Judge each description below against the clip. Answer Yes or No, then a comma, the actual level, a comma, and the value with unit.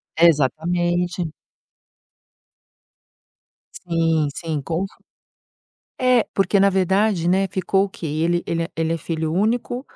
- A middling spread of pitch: Yes, average, 3.0 semitones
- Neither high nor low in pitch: Yes, medium, 175 Hz